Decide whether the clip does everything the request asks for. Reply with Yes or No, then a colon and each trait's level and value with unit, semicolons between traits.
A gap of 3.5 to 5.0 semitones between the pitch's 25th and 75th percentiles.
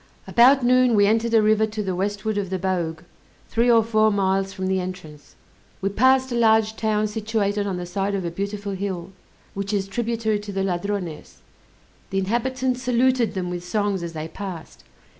No: average, 3.0 semitones